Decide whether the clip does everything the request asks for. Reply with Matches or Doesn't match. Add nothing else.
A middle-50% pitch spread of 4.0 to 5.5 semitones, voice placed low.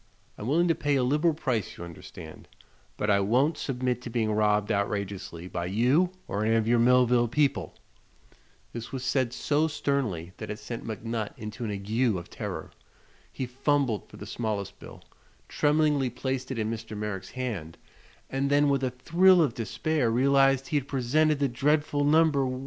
Matches